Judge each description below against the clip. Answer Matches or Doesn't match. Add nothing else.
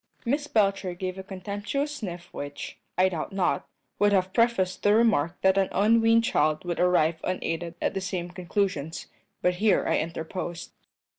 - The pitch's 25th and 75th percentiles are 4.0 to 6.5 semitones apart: Doesn't match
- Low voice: Doesn't match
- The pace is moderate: Matches